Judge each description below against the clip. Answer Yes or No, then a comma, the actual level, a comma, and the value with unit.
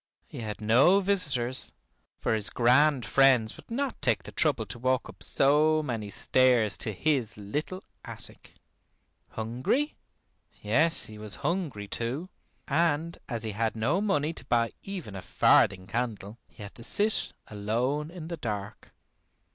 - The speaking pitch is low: Yes, low, 125 Hz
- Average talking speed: Yes, average, 150 wpm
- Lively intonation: Yes, wide, 6.1 semitones